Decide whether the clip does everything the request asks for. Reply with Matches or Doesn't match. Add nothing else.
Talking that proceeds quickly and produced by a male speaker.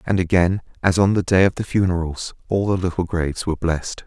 Matches